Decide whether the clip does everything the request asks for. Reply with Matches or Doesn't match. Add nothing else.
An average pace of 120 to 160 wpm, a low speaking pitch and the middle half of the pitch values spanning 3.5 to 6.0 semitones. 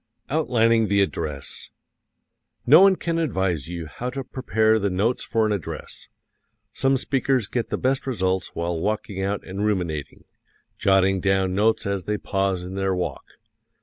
Matches